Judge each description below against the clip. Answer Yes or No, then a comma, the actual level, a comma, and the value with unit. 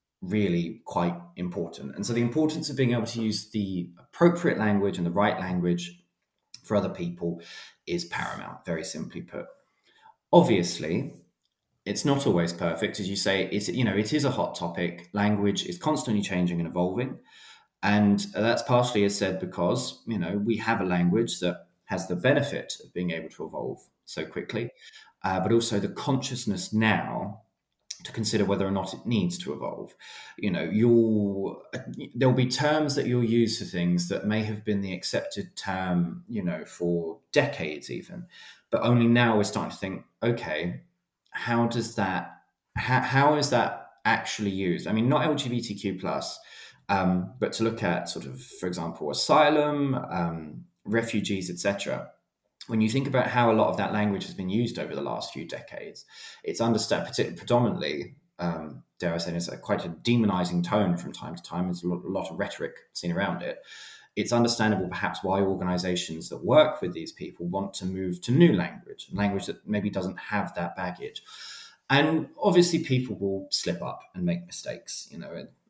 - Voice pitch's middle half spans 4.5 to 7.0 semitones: Yes, average, 5.2 semitones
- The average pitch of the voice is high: No, low, 105 Hz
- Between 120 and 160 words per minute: No, average, 180 wpm